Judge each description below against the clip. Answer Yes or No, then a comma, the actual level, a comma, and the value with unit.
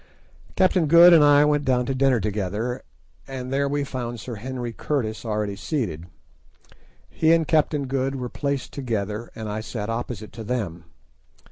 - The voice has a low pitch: Yes, low, 125 Hz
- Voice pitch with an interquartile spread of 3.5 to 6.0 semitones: Yes, average, 4.5 semitones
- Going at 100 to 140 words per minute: No, average, 160 wpm